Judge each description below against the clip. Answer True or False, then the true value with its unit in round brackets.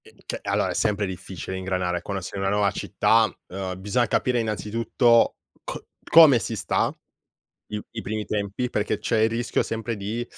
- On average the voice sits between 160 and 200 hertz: False (105 Hz)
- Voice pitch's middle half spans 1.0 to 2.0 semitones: False (2.8 semitones)